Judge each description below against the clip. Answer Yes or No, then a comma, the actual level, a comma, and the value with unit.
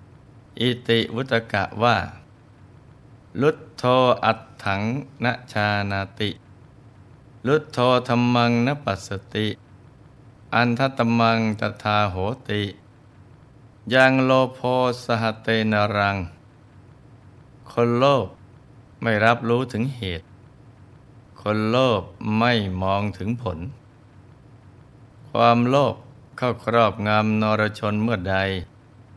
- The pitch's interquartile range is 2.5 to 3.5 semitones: Yes, average, 3.0 semitones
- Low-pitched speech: Yes, low, 115 Hz